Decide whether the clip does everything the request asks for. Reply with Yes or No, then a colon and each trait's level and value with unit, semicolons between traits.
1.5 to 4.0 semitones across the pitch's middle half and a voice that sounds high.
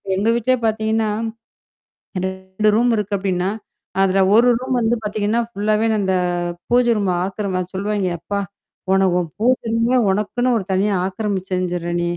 Yes: average, 2.9 semitones; high, 205 Hz